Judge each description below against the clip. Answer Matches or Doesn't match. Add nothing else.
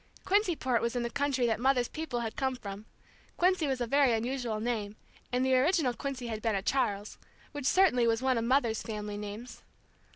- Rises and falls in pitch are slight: Doesn't match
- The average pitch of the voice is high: Matches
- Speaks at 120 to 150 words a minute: Doesn't match